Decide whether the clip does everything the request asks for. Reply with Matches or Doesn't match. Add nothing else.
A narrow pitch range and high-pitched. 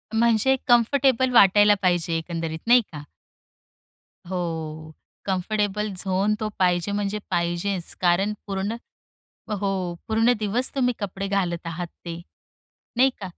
Doesn't match